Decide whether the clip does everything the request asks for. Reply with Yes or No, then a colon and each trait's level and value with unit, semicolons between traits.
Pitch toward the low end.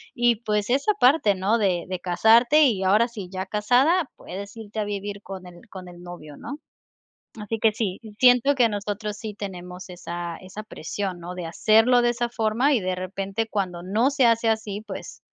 No: high, 210 Hz